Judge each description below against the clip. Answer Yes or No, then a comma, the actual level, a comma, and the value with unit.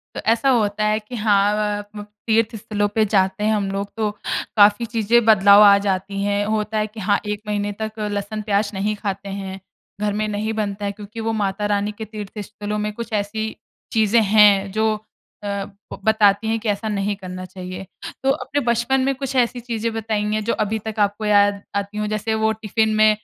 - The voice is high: Yes, high, 210 Hz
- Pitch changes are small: Yes, narrow, 1.4 semitones